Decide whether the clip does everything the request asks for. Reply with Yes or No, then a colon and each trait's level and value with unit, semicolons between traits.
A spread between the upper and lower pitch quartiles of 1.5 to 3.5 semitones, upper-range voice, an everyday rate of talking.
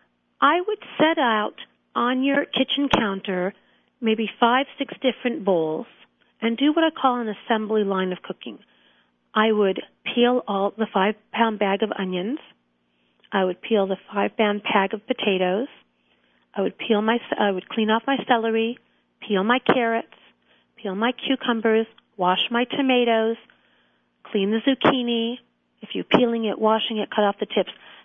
No: average, 3.9 semitones; high, 220 Hz; average, 160 wpm